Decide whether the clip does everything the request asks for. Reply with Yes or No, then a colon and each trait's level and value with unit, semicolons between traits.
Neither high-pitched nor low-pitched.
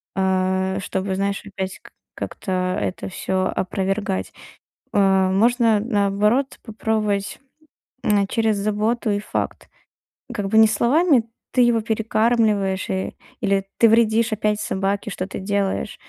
No: high, 205 Hz